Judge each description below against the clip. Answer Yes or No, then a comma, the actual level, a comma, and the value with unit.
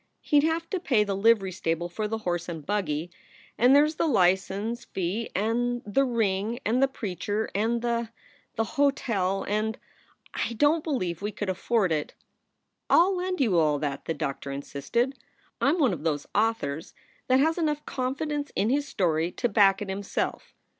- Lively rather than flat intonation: Yes, wide, 6.3 semitones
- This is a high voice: Yes, high, 215 Hz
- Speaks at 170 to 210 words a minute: Yes, average, 190 wpm